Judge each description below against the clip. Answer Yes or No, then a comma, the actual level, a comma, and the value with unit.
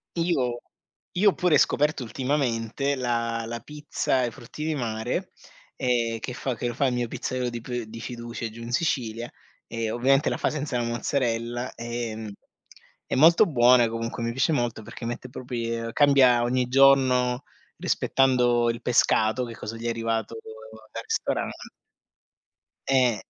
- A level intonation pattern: Yes, narrow, 2.3 semitones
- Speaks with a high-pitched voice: No, low, 120 Hz